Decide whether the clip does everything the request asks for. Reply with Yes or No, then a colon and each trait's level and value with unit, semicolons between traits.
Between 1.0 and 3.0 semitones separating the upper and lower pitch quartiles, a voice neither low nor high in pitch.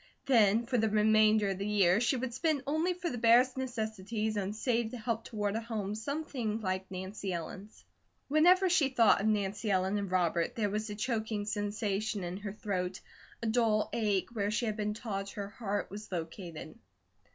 No: average, 2.7 semitones; high, 215 Hz